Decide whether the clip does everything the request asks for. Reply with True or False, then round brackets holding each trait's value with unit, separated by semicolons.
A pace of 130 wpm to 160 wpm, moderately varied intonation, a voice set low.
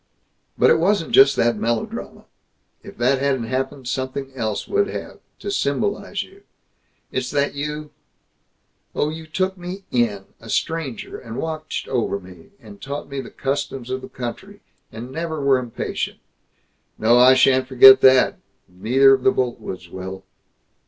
True (150 wpm; 4.1 semitones; 130 Hz)